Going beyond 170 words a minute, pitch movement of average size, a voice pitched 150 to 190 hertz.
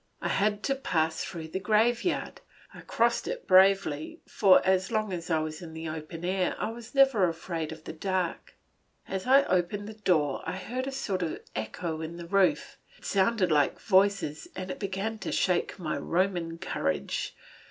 Yes: average, 185 wpm; average, 4.0 semitones; medium, 185 Hz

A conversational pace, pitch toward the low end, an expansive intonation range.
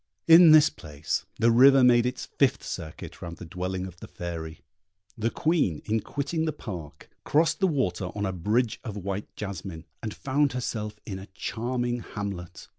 Yes: average, 175 wpm; low, 110 Hz; wide, 6.2 semitones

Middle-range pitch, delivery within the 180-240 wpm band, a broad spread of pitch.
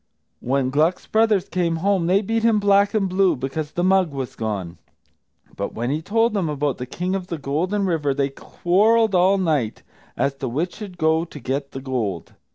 Yes: medium, 165 Hz; average, 195 wpm; wide, 6.0 semitones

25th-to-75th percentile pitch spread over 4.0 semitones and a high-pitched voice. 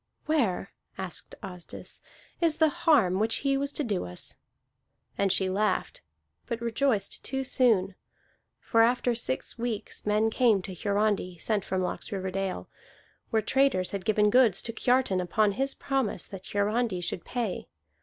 Yes: average, 4.5 semitones; high, 215 Hz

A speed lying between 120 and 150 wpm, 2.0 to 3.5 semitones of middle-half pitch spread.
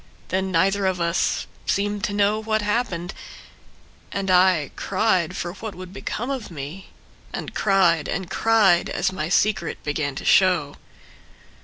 Yes: average, 145 wpm; average, 3.1 semitones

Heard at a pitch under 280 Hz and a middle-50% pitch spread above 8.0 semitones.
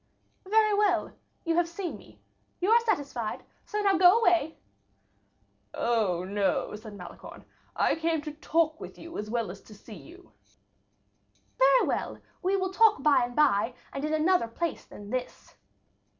No: very high, 320 Hz; wide, 8.4 semitones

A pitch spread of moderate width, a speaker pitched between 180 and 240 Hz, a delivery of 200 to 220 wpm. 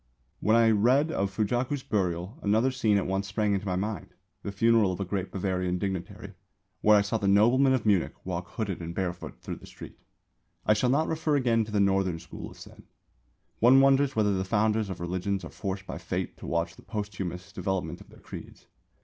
No: average, 3.3 semitones; low, 100 Hz; fast, 205 wpm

